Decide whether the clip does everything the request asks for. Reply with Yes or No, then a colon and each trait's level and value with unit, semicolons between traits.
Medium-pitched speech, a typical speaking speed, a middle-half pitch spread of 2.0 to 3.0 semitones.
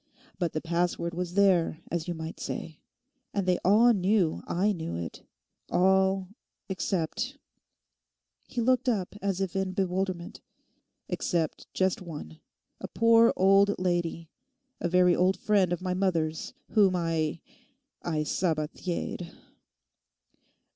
No: medium, 180 Hz; slow, 115 wpm; narrow, 2.6 semitones